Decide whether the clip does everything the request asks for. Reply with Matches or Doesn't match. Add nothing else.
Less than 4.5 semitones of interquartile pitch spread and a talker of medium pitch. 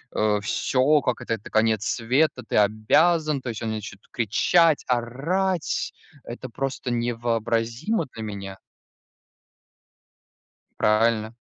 Doesn't match